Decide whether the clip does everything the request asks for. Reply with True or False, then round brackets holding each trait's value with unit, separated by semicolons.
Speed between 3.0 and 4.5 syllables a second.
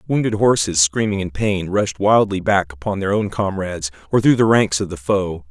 False (5.1 syllables/s)